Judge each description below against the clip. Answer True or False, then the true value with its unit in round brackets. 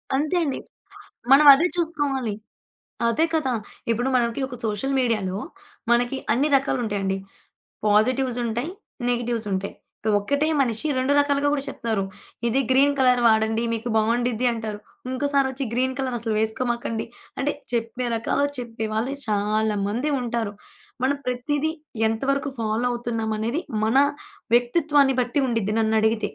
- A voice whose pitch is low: False (240 Hz)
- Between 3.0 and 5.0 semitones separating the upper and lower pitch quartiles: True (3.6 semitones)